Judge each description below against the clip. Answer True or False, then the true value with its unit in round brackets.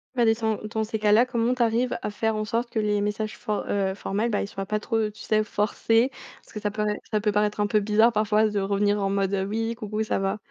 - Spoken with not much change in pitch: True (1.3 semitones)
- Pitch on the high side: True (215 Hz)